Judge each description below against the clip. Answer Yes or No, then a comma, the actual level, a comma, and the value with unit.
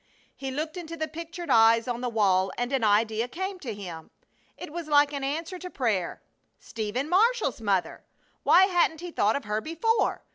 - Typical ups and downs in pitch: No, wide, 7.1 semitones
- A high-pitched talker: Yes, very high, 275 Hz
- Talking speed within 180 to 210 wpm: Yes, average, 185 wpm